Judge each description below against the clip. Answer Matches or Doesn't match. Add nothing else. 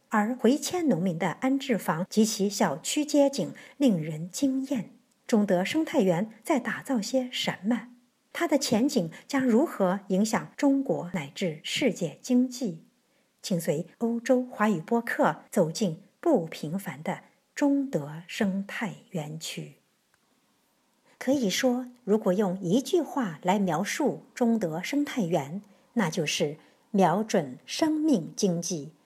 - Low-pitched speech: Doesn't match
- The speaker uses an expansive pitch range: Matches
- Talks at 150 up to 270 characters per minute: Matches